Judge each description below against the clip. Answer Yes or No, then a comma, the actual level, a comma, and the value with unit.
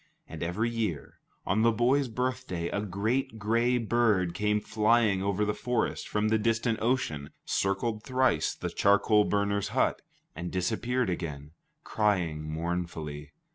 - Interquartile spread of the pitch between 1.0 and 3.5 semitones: No, average, 4.6 semitones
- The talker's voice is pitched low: Yes, low, 105 Hz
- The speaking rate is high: No, slow, 135 wpm